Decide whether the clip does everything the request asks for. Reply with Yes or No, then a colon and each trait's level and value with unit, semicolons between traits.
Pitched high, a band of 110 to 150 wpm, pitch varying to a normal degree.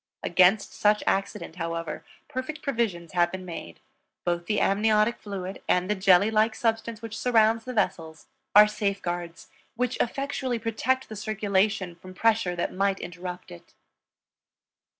Yes: high, 205 Hz; average, 140 wpm; average, 3.9 semitones